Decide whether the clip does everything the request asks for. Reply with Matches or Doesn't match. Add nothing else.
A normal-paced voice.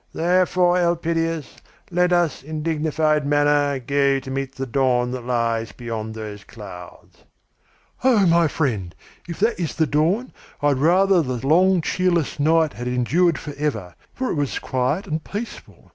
Matches